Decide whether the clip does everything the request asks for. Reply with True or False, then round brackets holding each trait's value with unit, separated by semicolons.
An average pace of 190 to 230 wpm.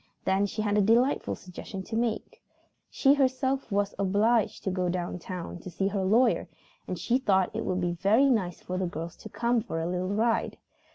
True (205 wpm)